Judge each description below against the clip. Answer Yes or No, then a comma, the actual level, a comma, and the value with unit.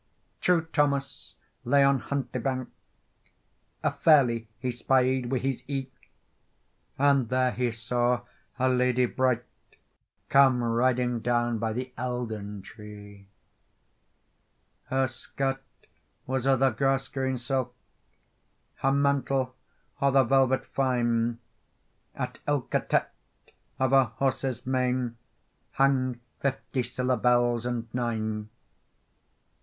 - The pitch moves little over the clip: Yes, narrow, 1.9 semitones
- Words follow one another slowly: Yes, slow, 110 wpm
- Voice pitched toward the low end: Yes, low, 125 Hz